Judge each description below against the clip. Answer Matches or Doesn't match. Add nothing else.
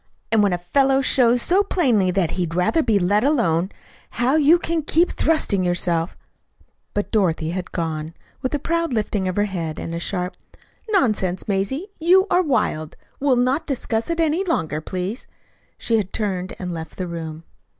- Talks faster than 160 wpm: Matches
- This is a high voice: Matches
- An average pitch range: Doesn't match